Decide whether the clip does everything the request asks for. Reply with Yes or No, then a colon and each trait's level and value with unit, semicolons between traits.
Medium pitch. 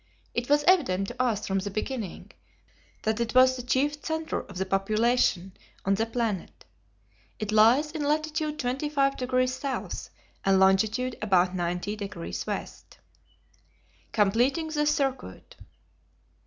No: high, 240 Hz